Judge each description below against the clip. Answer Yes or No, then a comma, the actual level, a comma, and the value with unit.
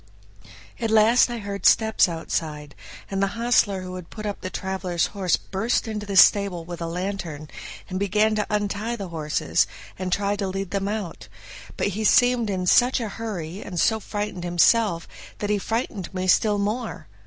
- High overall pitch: Yes, high, 200 Hz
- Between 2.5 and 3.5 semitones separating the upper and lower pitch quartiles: Yes, average, 3.0 semitones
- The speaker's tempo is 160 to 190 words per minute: Yes, average, 180 wpm